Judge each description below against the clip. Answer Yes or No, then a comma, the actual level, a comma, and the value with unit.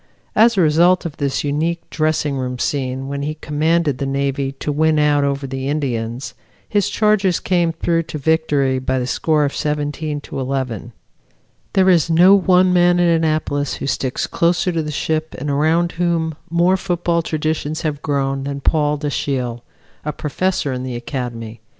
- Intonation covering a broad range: No, average, 3.5 semitones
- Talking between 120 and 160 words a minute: No, average, 170 wpm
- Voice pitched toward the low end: No, medium, 150 Hz